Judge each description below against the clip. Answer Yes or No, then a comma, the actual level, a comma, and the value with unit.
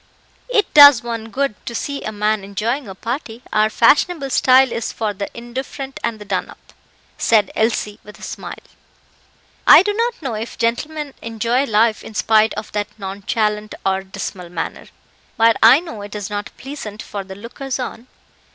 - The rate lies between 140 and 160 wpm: No, average, 175 wpm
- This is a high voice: Yes, high, 225 Hz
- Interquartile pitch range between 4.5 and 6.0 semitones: No, average, 4.0 semitones